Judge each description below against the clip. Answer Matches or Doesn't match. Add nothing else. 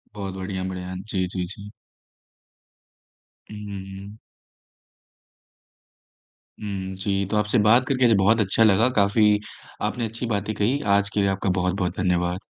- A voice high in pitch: Doesn't match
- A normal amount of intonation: Doesn't match